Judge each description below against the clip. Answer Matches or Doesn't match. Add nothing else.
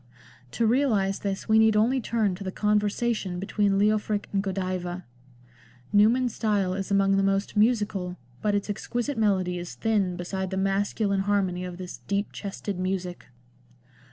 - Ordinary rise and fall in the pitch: Doesn't match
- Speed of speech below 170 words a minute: Matches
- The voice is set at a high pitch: Matches